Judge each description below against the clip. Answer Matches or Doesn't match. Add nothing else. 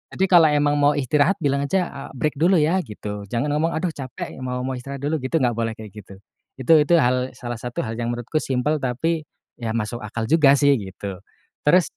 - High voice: Doesn't match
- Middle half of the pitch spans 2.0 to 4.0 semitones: Doesn't match